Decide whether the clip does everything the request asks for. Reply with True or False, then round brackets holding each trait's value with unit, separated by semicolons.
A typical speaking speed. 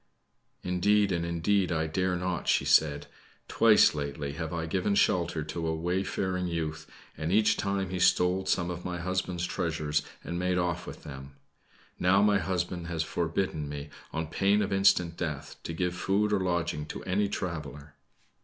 True (170 wpm)